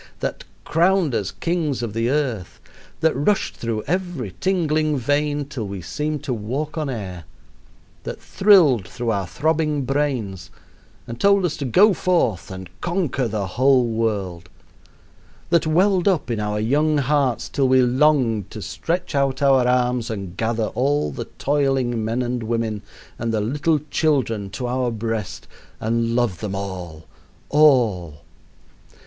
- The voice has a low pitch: Yes, low, 125 Hz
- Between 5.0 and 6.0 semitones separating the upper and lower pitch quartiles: Yes, wide, 5.5 semitones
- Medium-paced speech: Yes, average, 150 wpm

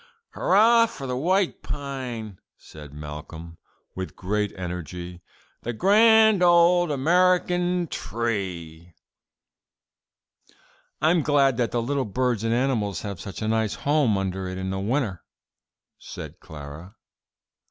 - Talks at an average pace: No, slow, 120 wpm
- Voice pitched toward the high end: No, low, 115 Hz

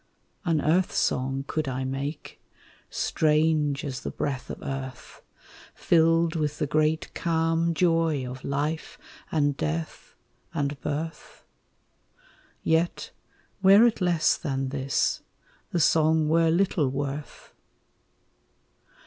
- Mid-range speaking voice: Yes, medium, 155 Hz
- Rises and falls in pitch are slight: No, average, 3.0 semitones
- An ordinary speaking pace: No, slow, 110 wpm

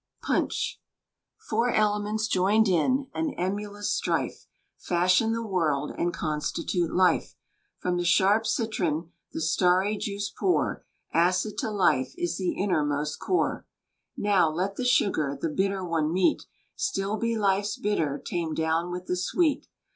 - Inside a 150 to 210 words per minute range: No, average, 140 wpm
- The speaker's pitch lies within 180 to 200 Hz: Yes, high, 190 Hz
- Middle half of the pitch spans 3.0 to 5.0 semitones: Yes, average, 4.0 semitones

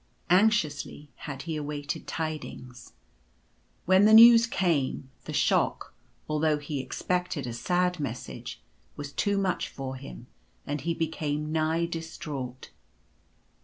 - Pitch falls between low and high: Yes, medium, 155 Hz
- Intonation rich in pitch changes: No, average, 3.9 semitones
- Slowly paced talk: Yes, slow, 120 wpm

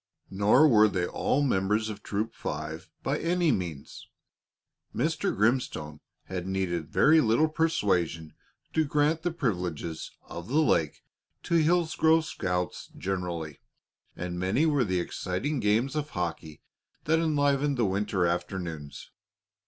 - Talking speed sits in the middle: No, slow, 130 wpm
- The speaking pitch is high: No, low, 105 Hz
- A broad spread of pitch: Yes, wide, 9.0 semitones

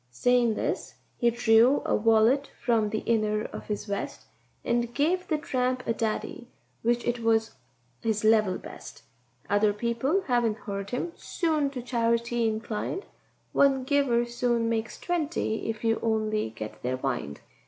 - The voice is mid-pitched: No, high, 230 Hz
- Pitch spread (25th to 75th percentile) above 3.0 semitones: No, narrow, 2.5 semitones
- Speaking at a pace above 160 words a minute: No, average, 150 wpm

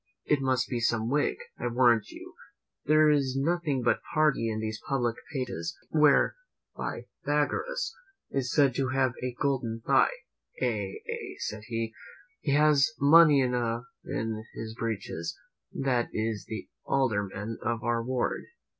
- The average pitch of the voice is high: No, low, 125 Hz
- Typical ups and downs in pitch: Yes, average, 3.7 semitones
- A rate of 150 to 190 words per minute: No, average, 140 wpm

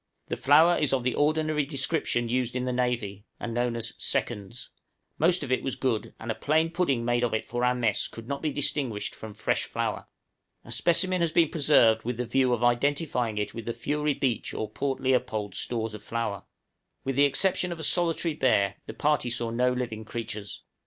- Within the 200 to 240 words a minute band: Yes, fast, 205 wpm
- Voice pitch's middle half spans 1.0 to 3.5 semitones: No, average, 4.2 semitones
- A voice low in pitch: Yes, low, 125 Hz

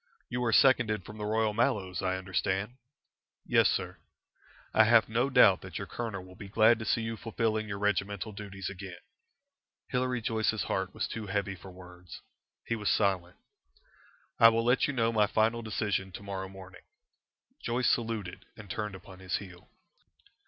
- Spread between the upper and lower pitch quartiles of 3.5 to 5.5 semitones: No, average, 3.0 semitones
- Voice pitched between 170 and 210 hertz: No, low, 105 Hz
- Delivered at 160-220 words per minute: Yes, average, 170 wpm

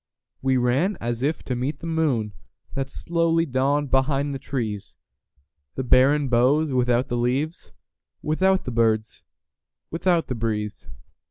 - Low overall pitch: Yes, low, 130 Hz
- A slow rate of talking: Yes, slow, 120 wpm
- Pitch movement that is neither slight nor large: Yes, average, 4.1 semitones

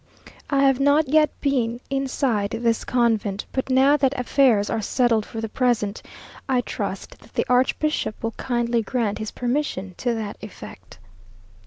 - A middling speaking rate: Yes, average, 155 wpm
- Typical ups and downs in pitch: Yes, average, 3.5 semitones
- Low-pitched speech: No, high, 245 Hz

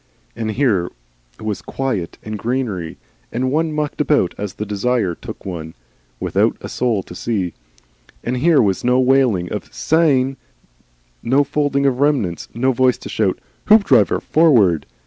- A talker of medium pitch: No, low, 125 Hz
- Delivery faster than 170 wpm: No, average, 145 wpm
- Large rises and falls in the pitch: Yes, wide, 5.7 semitones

